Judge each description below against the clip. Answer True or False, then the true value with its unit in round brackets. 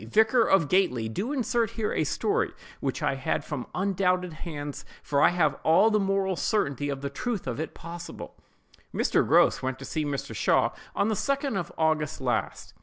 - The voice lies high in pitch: False (175 Hz)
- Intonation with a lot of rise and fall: True (6.6 semitones)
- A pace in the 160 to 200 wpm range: True (185 wpm)